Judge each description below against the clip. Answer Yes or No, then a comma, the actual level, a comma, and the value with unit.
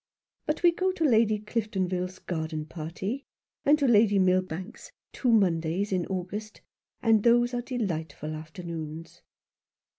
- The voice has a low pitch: No, high, 195 Hz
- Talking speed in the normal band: No, slow, 125 wpm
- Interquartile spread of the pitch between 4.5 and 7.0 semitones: Yes, wide, 5.6 semitones